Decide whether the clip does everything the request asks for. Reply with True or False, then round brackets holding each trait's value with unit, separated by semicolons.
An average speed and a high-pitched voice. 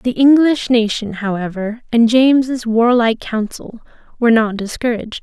False (125 wpm; 230 Hz)